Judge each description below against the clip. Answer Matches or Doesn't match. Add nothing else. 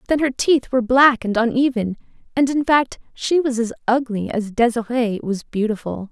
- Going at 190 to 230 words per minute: Doesn't match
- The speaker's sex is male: Doesn't match